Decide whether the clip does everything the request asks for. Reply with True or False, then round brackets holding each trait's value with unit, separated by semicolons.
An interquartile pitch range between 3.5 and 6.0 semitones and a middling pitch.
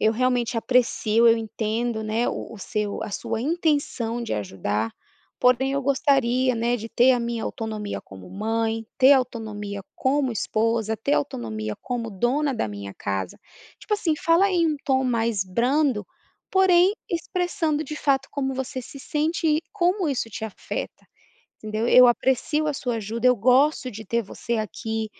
False (4.1 semitones; 240 Hz)